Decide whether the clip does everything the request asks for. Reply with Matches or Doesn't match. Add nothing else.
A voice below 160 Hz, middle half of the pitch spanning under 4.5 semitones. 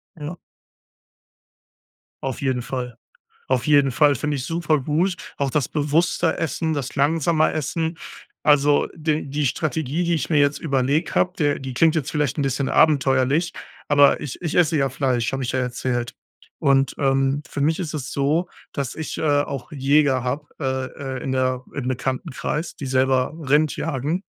Matches